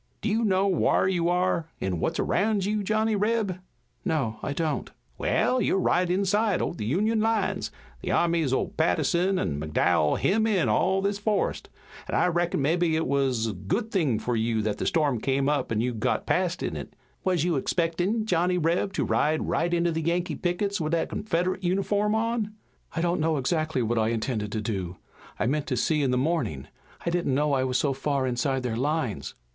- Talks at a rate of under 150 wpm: No, average, 200 wpm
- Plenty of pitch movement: Yes, wide, 6.4 semitones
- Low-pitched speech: No, medium, 165 Hz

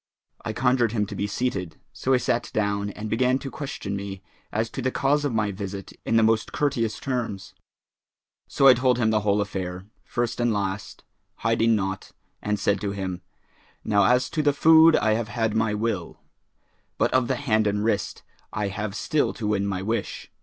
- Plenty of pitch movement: No, average, 3.5 semitones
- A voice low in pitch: Yes, low, 110 Hz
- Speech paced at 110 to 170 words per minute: No, average, 195 wpm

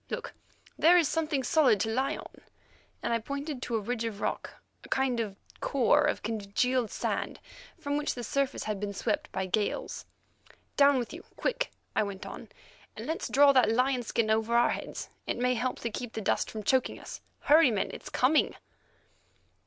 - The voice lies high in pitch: Yes, high, 245 Hz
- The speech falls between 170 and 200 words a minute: Yes, average, 190 wpm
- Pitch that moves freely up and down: No, average, 4.2 semitones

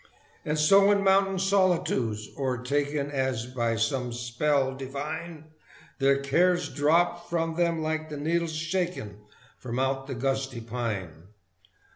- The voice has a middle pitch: Yes, medium, 145 Hz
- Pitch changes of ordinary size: Yes, average, 5.0 semitones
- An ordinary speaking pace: No, slow, 125 wpm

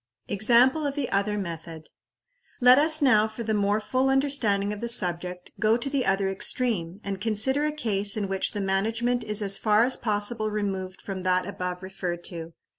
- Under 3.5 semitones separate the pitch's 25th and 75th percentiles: No, average, 3.8 semitones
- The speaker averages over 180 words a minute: Yes, average, 190 wpm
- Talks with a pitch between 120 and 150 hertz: No, high, 210 Hz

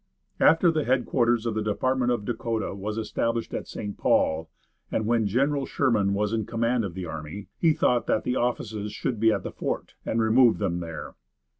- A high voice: No, low, 115 Hz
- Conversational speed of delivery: Yes, average, 190 wpm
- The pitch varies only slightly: No, average, 3.1 semitones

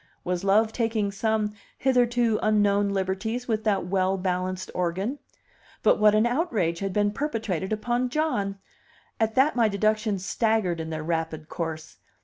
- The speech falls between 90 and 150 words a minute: Yes, average, 145 wpm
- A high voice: Yes, high, 205 Hz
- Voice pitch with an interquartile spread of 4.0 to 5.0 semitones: No, average, 3.3 semitones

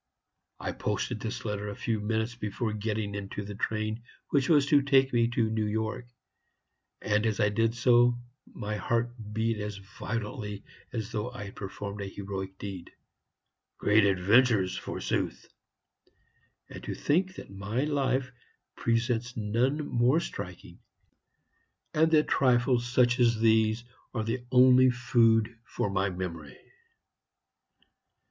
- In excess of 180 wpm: No, slow, 135 wpm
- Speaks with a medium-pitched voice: No, low, 110 Hz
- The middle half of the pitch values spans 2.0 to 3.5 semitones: Yes, average, 3.1 semitones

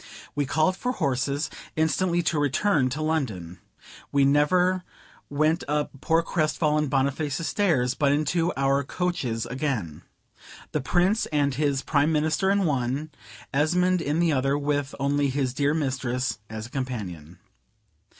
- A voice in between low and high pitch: Yes, medium, 145 Hz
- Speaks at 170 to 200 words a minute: No, average, 140 wpm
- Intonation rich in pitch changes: No, average, 3.2 semitones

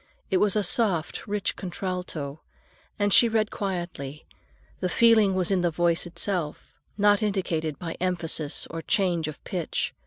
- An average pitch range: Yes, average, 3.6 semitones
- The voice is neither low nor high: Yes, medium, 180 Hz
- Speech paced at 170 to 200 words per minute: No, average, 150 wpm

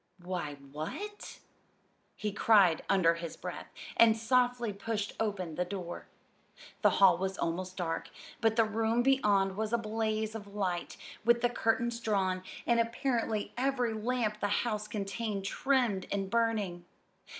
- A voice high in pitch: Yes, high, 215 Hz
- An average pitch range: Yes, average, 3.5 semitones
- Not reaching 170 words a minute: Yes, average, 145 wpm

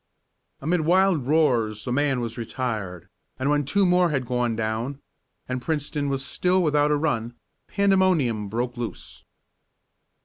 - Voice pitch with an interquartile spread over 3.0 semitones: Yes, average, 5.0 semitones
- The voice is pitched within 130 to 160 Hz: Yes, low, 135 Hz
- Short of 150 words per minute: Yes, average, 140 wpm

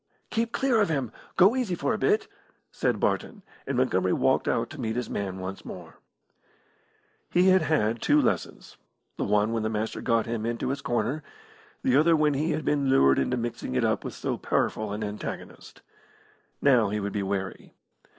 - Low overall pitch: Yes, low, 120 Hz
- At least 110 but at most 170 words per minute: No, average, 190 wpm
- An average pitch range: No, wide, 6.9 semitones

